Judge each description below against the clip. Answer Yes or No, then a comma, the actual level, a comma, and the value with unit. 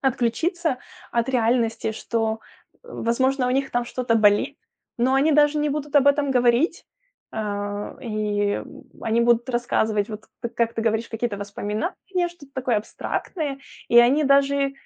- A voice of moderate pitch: No, high, 240 Hz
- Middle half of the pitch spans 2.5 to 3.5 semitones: No, average, 3.9 semitones